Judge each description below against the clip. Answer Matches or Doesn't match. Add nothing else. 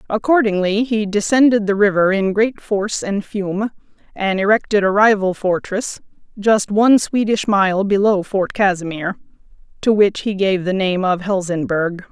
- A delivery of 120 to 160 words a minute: Matches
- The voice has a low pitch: Doesn't match